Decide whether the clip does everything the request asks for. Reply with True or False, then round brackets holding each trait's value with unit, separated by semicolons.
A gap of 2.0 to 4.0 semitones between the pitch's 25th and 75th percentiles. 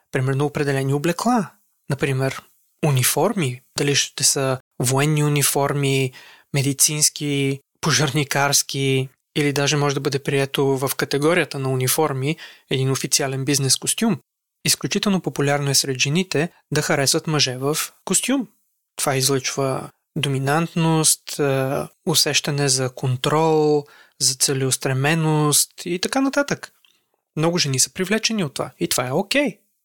True (2.8 semitones)